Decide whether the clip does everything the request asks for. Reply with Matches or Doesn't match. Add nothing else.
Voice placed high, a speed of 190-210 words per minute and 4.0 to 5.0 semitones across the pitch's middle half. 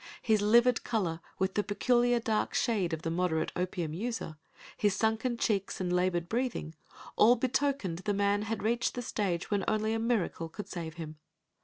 Doesn't match